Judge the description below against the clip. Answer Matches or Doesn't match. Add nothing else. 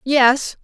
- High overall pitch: Matches